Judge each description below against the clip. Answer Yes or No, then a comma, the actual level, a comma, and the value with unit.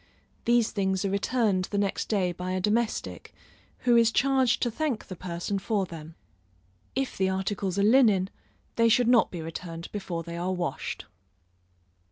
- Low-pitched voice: No, high, 200 Hz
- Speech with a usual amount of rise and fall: Yes, average, 4.1 semitones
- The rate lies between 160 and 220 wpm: Yes, average, 165 wpm